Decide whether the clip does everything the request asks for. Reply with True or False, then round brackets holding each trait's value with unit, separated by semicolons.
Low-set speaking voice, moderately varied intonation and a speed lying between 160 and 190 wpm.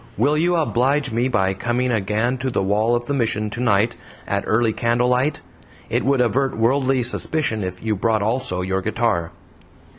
True (120 Hz; 3.5 semitones; 170 wpm)